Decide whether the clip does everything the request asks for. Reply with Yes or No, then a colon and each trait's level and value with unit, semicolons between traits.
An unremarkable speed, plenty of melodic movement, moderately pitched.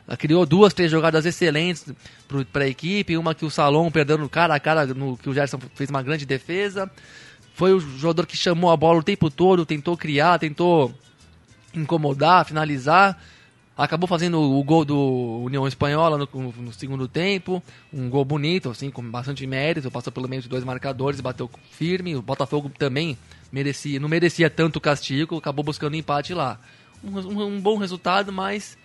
No: average, 175 wpm; average, 4.0 semitones; medium, 150 Hz